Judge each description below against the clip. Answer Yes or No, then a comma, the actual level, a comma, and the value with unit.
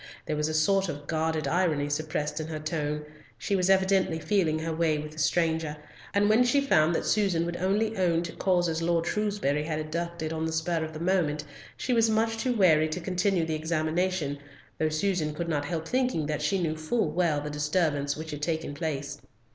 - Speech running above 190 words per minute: Yes, fast, 205 wpm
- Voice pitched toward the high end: No, medium, 160 Hz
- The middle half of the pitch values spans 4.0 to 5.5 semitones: No, average, 3.2 semitones